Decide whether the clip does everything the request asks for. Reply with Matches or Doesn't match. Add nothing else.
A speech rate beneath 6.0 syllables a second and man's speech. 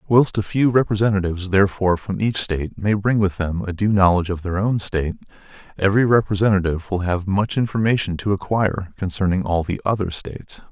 Doesn't match